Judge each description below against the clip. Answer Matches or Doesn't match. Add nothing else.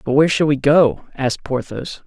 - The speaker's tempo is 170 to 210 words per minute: Matches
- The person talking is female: Doesn't match